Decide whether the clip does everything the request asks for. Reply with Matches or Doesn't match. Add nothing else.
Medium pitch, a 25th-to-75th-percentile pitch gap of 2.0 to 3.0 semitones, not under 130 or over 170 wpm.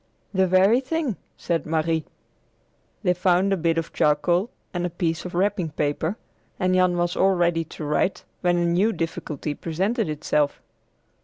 Matches